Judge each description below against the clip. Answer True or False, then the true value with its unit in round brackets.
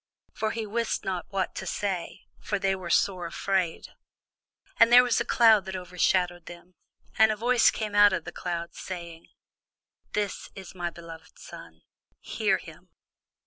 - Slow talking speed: False (160 wpm)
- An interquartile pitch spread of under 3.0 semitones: False (3.3 semitones)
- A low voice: False (190 Hz)